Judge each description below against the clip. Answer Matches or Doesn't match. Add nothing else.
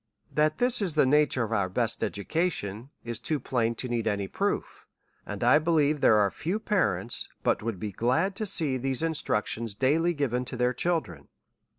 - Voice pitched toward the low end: Matches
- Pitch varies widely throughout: Matches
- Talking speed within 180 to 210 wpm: Matches